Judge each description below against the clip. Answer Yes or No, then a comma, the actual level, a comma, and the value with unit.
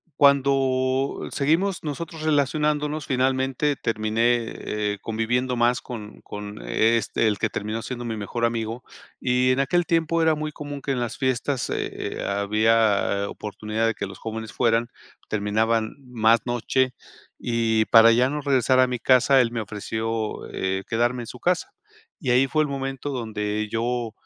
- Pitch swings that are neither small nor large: Yes, average, 3.4 semitones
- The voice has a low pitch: Yes, low, 120 Hz